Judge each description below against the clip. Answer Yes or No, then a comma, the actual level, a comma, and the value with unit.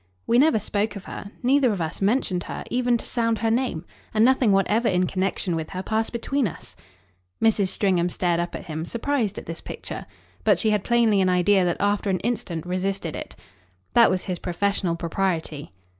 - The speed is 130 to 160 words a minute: No, average, 195 wpm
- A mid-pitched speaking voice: No, high, 200 Hz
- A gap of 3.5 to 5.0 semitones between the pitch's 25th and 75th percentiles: Yes, average, 4.2 semitones